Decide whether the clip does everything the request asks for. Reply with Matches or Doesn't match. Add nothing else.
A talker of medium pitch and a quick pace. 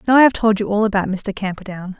Doesn't match